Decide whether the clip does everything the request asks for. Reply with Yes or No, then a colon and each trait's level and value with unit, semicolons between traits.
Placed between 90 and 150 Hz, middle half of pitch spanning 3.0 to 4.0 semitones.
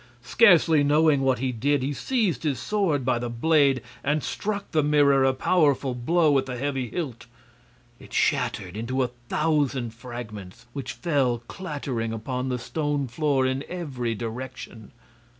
Yes: low, 135 Hz; average, 3.6 semitones